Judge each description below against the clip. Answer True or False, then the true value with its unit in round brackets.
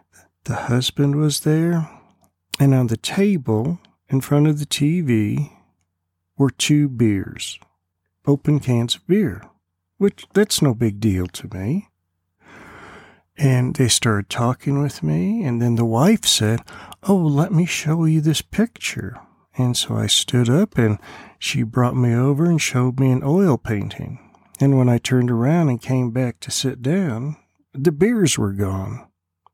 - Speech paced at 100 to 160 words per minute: True (155 wpm)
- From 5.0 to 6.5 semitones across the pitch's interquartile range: True (5.5 semitones)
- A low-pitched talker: True (130 Hz)